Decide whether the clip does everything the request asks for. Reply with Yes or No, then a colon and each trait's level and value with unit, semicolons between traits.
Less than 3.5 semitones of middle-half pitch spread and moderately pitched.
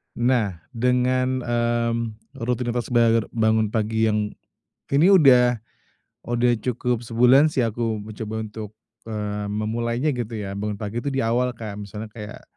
No: narrow, 2.4 semitones; low, 115 Hz